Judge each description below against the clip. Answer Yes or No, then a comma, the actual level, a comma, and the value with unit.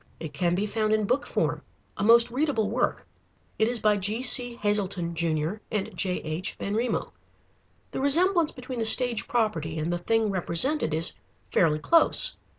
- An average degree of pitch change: No, wide, 5.8 semitones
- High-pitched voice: Yes, high, 215 Hz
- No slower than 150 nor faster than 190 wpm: Yes, average, 155 wpm